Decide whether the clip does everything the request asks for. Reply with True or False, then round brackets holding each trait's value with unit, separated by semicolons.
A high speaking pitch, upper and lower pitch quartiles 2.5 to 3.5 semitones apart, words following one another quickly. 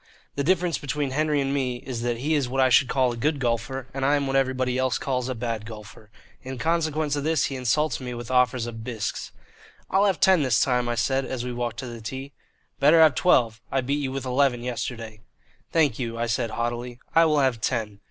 False (130 Hz; 2.9 semitones; 230 wpm)